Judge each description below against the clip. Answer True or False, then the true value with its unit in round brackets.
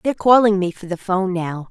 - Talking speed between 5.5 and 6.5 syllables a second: True (6.3 syllables/s)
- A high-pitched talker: True (195 Hz)